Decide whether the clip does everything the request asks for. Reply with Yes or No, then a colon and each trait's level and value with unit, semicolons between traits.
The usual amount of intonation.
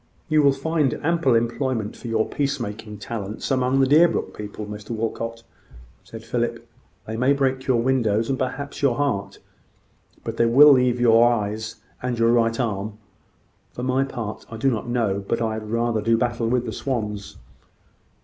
Yes: average, 3.1 semitones